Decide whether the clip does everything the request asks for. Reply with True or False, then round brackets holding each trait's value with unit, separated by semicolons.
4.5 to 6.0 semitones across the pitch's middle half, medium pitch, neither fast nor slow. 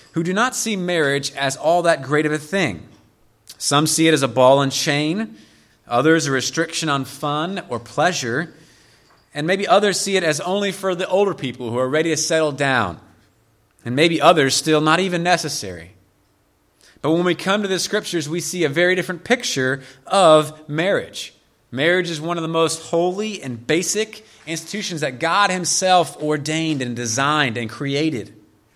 True (5.3 semitones; 155 Hz; 175 wpm)